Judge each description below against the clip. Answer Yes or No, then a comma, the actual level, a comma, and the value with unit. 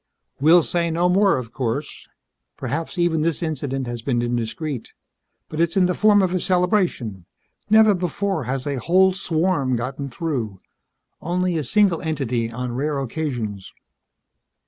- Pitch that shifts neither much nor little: No, wide, 6.1 semitones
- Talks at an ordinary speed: Yes, average, 145 wpm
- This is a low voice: No, medium, 155 Hz